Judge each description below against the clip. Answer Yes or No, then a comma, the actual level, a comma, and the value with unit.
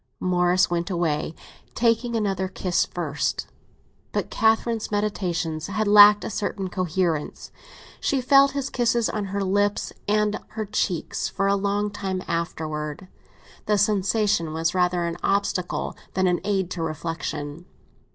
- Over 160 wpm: No, average, 140 wpm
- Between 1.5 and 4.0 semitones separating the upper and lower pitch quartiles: Yes, average, 3.5 semitones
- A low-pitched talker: No, high, 190 Hz